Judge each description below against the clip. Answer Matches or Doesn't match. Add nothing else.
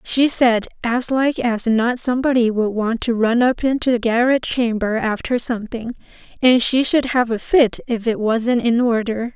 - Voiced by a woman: Matches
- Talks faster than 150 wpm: Matches